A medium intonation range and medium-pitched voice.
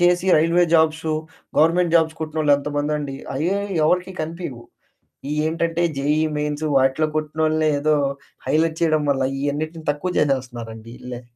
No: narrow, 2.2 semitones; medium, 155 Hz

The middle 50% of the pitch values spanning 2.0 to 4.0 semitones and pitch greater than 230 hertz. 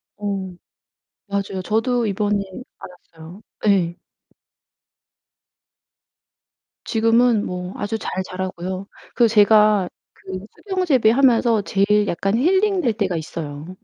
No: average, 3.5 semitones; high, 205 Hz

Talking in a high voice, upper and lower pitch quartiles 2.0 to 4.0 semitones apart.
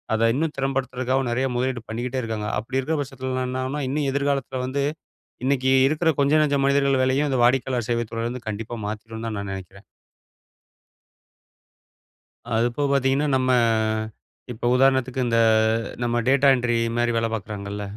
No: low, 130 Hz; average, 2.8 semitones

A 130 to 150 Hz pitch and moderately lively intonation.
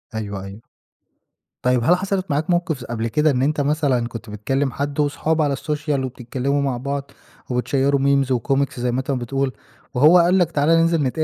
Yes: medium, 140 Hz; average, 3.3 semitones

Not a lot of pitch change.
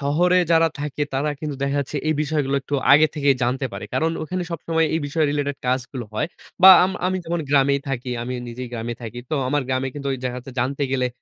No: average, 3.2 semitones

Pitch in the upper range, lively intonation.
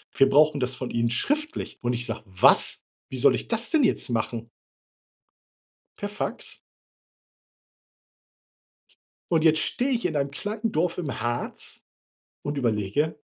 No: medium, 145 Hz; wide, 8.9 semitones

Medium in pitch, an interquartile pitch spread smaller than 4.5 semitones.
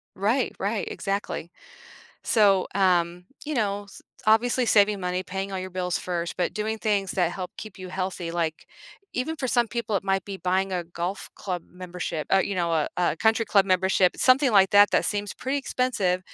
No: high, 195 Hz; average, 3.0 semitones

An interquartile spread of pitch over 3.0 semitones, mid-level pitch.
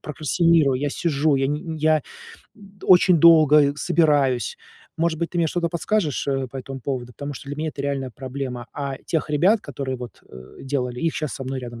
Yes: average, 3.4 semitones; medium, 145 Hz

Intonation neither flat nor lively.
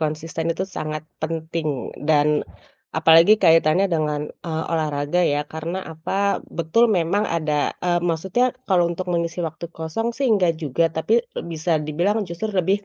No: narrow, 2.3 semitones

